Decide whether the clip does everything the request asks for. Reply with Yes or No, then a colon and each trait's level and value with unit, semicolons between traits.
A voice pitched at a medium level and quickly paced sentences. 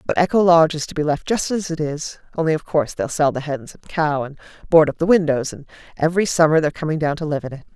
Yes: medium, 155 Hz; fast, 270 wpm